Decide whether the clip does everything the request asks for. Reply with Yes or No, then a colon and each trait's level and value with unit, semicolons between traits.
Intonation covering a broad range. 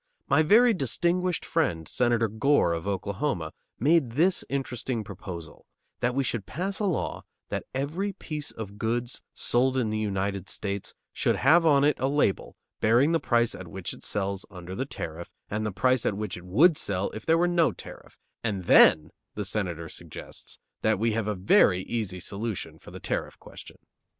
Yes: wide, 6.7 semitones